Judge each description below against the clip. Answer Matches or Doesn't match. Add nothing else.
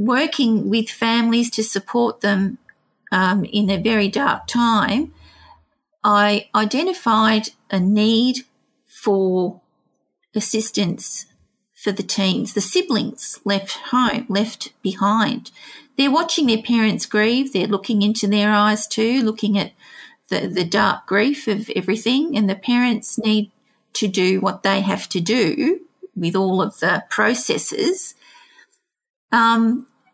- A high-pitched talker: Matches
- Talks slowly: Matches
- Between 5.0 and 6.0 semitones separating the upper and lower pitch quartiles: Doesn't match